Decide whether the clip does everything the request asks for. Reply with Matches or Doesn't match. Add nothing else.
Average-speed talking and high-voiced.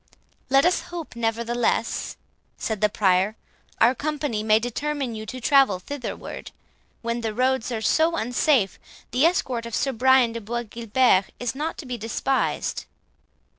Matches